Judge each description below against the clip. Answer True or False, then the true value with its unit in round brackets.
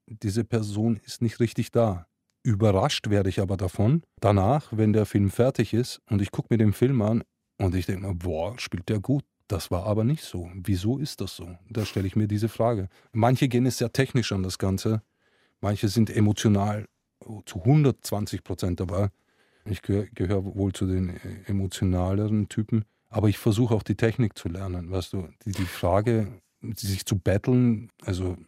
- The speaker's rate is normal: True (180 wpm)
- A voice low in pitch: True (105 Hz)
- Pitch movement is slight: False (3.2 semitones)